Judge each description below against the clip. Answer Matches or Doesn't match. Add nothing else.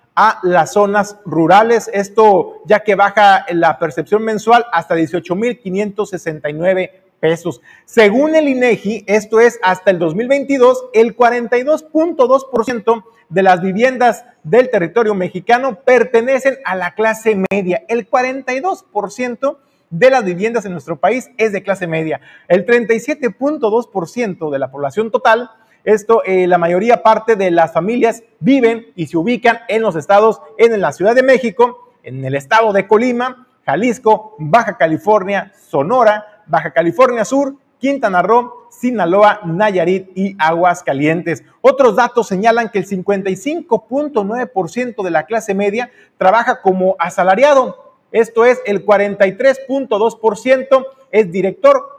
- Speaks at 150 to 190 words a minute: Doesn't match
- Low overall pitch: Doesn't match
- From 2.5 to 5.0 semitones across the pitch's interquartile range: Matches